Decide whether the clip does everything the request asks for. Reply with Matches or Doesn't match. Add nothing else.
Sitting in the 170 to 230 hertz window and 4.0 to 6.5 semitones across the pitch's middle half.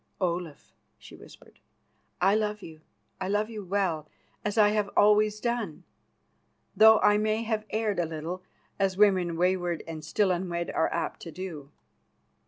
Doesn't match